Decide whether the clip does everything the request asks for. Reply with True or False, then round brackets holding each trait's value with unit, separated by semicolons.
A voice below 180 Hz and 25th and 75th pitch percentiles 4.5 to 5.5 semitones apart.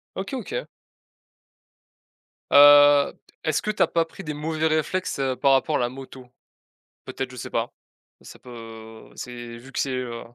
False (140 Hz; 3.7 semitones)